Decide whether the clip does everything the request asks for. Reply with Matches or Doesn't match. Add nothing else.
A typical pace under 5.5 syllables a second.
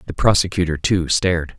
Doesn't match